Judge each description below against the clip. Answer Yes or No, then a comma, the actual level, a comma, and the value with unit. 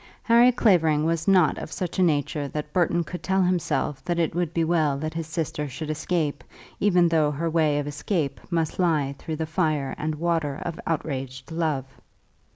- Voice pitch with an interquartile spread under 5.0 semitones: Yes, narrow, 2.6 semitones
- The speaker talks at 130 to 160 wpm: No, average, 185 wpm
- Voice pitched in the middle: Yes, medium, 160 Hz